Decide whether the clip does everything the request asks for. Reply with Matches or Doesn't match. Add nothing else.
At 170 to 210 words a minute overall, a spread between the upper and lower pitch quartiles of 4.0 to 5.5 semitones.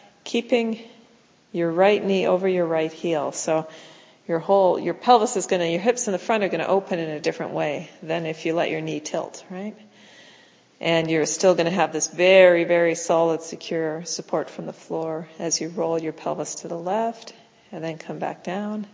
Doesn't match